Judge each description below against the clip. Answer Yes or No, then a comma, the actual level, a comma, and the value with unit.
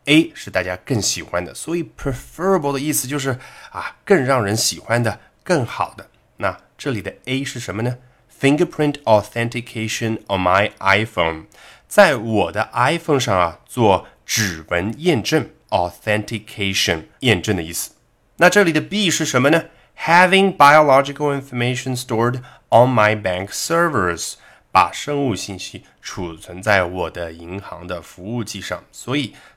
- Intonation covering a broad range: Yes, wide, 6.5 semitones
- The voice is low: Yes, low, 120 Hz